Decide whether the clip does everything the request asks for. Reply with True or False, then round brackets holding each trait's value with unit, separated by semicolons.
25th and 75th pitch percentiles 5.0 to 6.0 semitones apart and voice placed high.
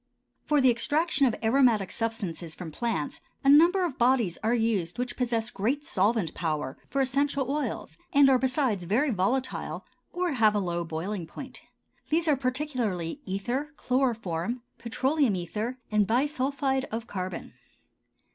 True (5.6 semitones; 240 Hz)